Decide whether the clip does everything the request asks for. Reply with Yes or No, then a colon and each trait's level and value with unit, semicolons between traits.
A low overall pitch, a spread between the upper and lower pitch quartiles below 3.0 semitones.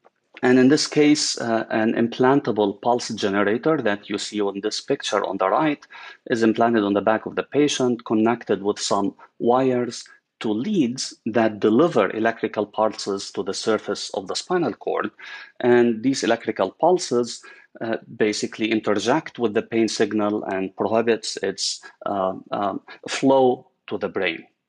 Yes: low, 115 Hz; narrow, 2.6 semitones